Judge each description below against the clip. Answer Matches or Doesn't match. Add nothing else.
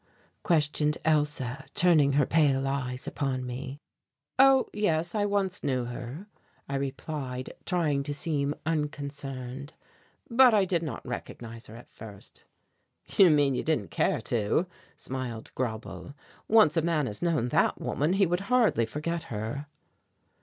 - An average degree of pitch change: Matches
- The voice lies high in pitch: Doesn't match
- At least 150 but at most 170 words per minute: Doesn't match